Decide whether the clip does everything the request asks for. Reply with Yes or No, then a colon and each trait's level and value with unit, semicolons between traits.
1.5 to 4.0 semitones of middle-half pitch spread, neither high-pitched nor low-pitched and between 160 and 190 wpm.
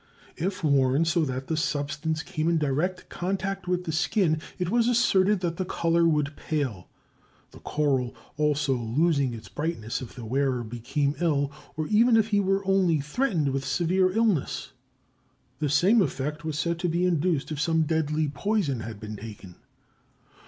No: average, 4.6 semitones; medium, 155 Hz; average, 165 wpm